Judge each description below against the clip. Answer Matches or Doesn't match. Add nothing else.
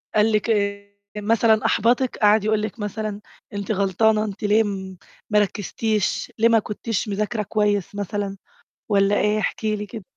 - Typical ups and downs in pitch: Doesn't match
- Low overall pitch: Doesn't match